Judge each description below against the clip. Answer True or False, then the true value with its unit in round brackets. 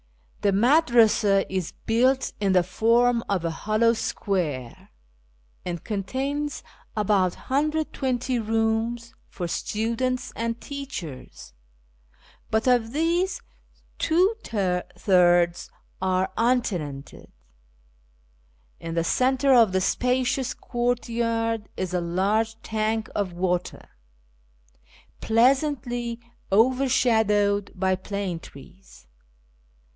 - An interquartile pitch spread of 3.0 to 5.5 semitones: True (4.8 semitones)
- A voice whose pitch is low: False (225 Hz)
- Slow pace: True (90 wpm)